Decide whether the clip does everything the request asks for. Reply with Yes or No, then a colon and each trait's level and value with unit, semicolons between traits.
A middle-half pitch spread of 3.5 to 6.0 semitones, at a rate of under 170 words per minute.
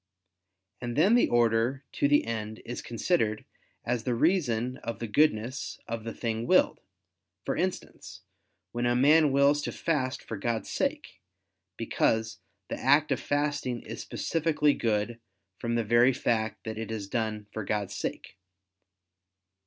Yes: average, 4.0 semitones; average, 150 wpm